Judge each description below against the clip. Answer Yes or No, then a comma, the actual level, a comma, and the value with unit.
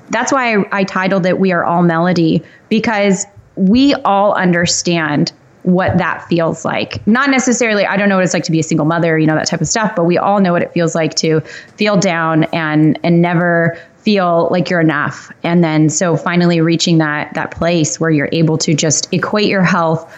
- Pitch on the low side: No, medium, 170 Hz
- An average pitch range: Yes, average, 3.0 semitones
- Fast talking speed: Yes, fast, 210 wpm